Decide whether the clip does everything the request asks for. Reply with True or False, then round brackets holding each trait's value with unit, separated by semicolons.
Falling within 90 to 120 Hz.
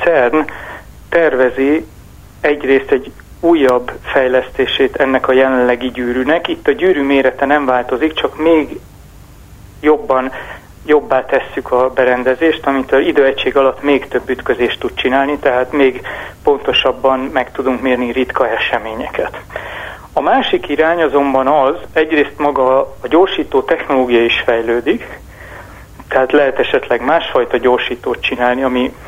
False (130 Hz)